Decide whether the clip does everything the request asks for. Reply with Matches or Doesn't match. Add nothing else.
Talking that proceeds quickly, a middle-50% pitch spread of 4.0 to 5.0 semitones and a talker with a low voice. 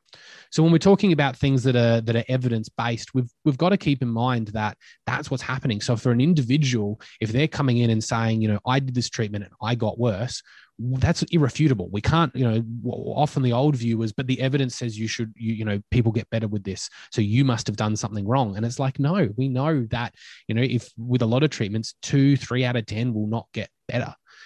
Doesn't match